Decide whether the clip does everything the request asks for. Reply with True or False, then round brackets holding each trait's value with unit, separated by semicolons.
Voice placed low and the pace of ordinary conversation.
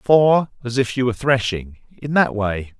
True (125 Hz; 170 wpm)